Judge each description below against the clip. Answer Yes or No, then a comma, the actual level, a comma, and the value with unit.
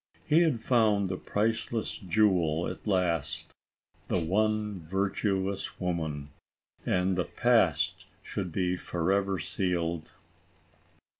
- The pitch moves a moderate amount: Yes, average, 3.3 semitones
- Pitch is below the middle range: Yes, very low, 95 Hz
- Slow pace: Yes, slow, 100 wpm